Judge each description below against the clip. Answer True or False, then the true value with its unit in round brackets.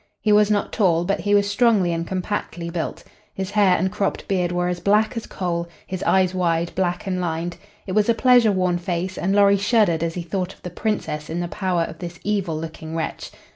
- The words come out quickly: True (220 wpm)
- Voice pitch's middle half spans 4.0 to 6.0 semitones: False (2.9 semitones)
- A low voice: False (185 Hz)